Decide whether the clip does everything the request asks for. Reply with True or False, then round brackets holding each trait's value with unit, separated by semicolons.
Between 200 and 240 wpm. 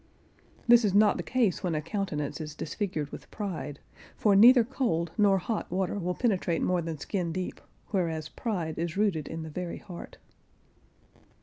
False (170 wpm)